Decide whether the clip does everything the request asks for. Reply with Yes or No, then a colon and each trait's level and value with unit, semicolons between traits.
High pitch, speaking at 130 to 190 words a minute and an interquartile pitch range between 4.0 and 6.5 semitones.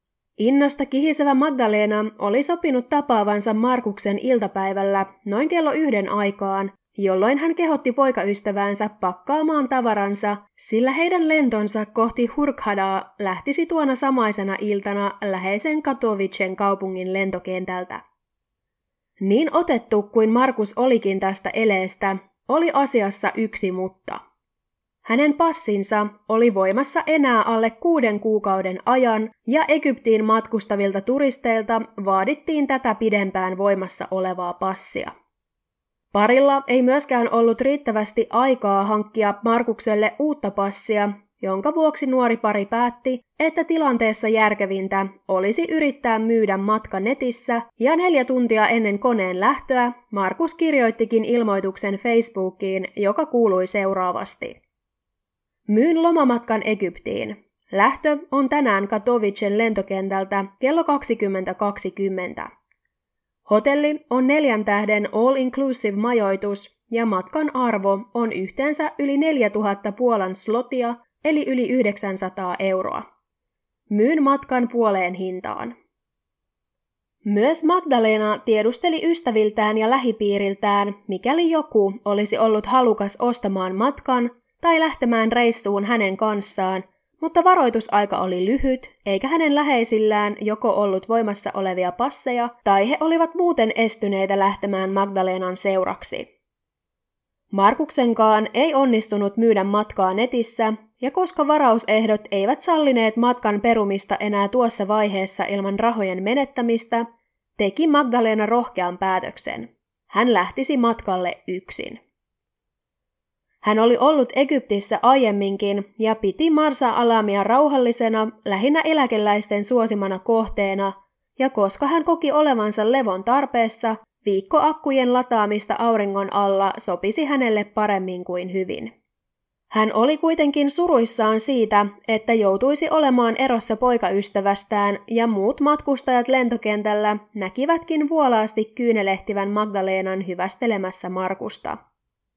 No: high, 220 Hz; average, 105 wpm; average, 4.5 semitones